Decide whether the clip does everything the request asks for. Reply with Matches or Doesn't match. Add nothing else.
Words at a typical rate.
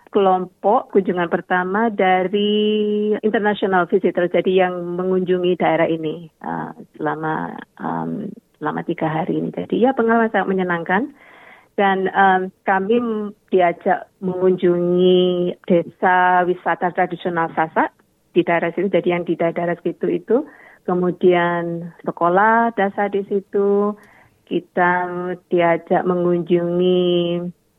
Matches